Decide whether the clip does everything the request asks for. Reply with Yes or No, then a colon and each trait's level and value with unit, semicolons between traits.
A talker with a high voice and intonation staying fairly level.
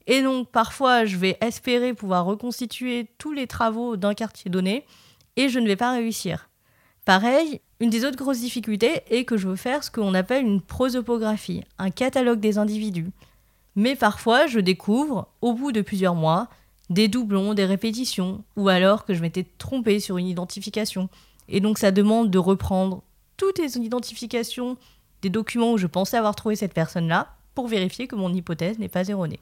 No: high, 215 Hz; average, 4.2 semitones